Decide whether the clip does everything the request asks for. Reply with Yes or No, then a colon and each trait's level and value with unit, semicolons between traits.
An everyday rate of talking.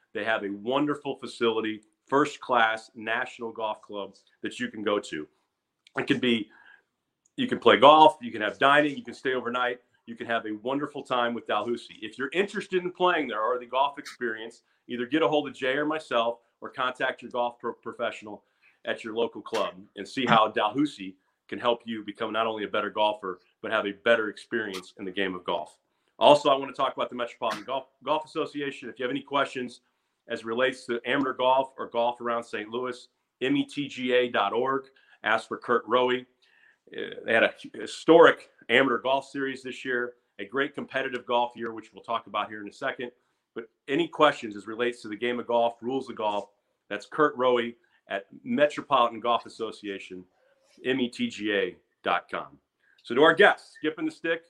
Yes: average, 190 wpm